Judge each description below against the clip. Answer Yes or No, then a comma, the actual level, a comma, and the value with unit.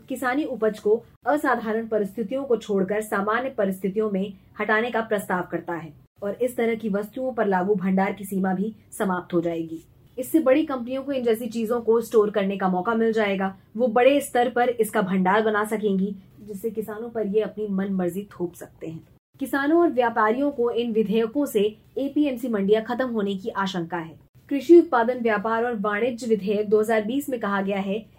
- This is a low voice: No, high, 220 Hz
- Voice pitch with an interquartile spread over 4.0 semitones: No, average, 3.5 semitones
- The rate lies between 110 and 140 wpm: No, average, 185 wpm